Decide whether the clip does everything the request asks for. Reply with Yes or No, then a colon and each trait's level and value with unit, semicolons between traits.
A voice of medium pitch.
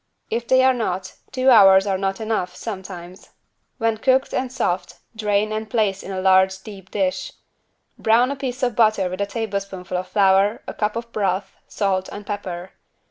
No: high, 205 Hz